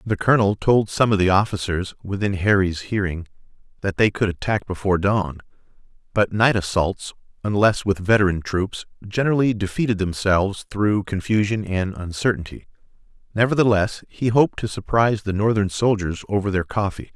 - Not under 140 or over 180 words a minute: Yes, average, 145 wpm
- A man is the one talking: Yes, male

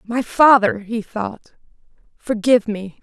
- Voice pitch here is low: No, high, 220 Hz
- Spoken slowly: Yes, slow, 120 wpm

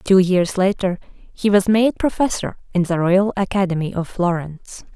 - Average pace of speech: Yes, average, 155 wpm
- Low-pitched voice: No, high, 190 Hz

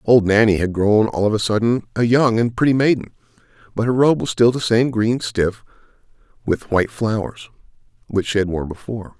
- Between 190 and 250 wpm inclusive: Yes, average, 195 wpm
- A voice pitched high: No, low, 110 Hz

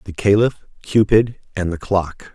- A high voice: No, low, 100 Hz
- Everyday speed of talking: Yes, average, 155 wpm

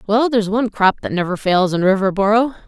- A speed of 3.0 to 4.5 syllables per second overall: No, 6.4 syllables/s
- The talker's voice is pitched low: No, high, 205 Hz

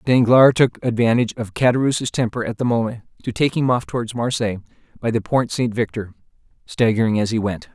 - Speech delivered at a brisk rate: No, average, 185 wpm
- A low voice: Yes, low, 115 Hz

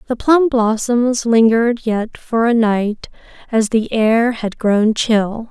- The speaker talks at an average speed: Yes, average, 150 wpm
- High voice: Yes, high, 230 Hz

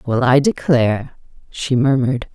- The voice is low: Yes, low, 130 Hz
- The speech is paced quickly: No, slow, 130 wpm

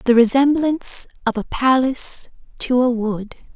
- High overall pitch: Yes, very high, 250 Hz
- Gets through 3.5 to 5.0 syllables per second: Yes, 4.7 syllables/s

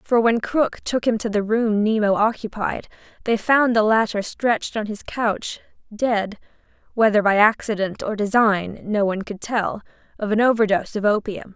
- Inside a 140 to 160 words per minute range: No, average, 170 wpm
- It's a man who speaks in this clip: No, female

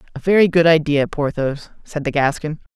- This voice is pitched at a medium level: Yes, medium, 155 Hz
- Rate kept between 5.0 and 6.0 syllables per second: Yes, 5.4 syllables/s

